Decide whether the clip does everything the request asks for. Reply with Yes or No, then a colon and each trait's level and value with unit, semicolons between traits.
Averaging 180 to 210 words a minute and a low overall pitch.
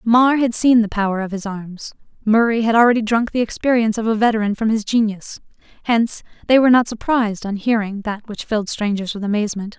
No: average, 200 wpm; high, 220 Hz